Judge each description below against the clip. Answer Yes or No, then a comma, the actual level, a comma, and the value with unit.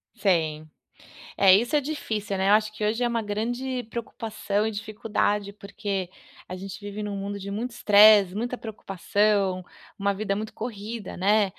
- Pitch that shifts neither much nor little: No, narrow, 1.9 semitones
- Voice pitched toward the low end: No, high, 210 Hz